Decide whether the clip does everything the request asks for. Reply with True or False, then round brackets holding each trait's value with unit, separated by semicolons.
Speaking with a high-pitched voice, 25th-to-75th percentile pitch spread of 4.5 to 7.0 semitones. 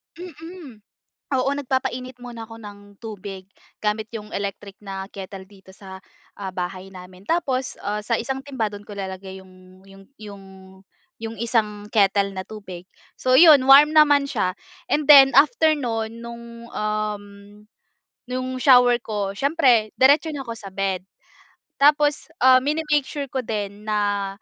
True (220 Hz; 5.0 semitones)